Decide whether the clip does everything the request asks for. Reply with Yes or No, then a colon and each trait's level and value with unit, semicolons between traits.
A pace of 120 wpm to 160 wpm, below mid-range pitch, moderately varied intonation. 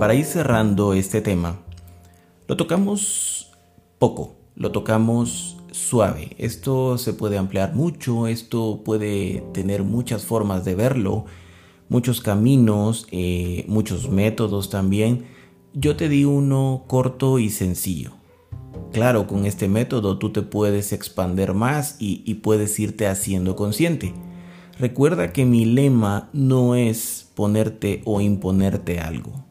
Yes: slow, 125 wpm; low, 105 Hz; average, 4.2 semitones